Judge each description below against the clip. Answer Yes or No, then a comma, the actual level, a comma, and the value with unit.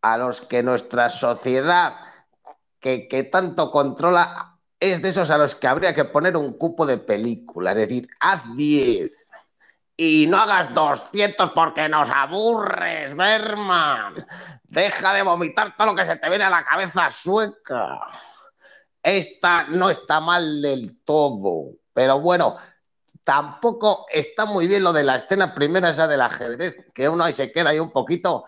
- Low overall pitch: No, medium, 170 Hz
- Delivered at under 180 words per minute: Yes, average, 160 wpm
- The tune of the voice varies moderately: Yes, average, 5.0 semitones